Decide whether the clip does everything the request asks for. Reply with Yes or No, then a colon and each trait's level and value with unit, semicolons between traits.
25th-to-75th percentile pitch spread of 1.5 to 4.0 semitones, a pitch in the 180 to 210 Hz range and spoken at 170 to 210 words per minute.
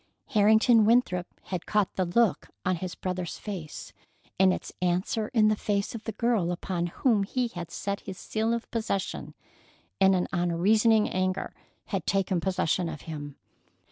No: average, 3.6 semitones; high, 190 Hz; average, 160 wpm